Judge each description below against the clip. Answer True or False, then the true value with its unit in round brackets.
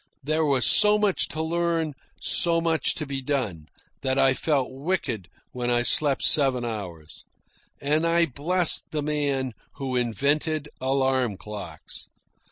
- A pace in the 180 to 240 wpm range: False (140 wpm)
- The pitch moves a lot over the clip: False (4.1 semitones)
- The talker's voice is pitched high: False (140 Hz)